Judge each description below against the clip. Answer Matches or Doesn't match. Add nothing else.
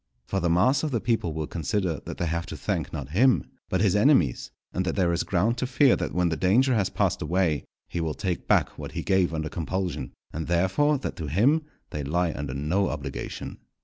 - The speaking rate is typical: Doesn't match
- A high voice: Doesn't match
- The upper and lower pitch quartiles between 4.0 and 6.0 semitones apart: Matches